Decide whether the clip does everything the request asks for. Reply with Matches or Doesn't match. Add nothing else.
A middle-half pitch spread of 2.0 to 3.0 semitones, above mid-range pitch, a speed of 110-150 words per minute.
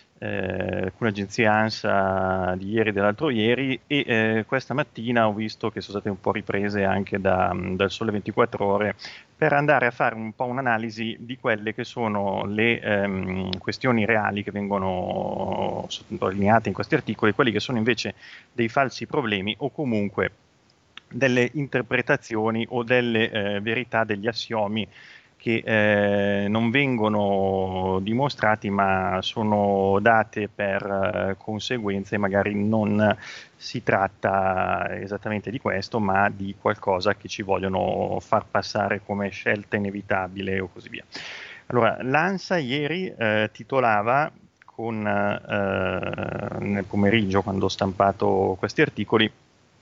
Doesn't match